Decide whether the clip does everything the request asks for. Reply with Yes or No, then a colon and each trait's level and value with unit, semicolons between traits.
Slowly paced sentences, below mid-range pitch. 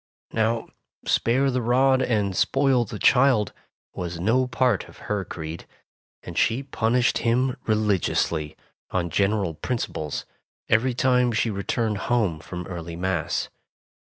Yes: slow, 130 wpm; low, 110 Hz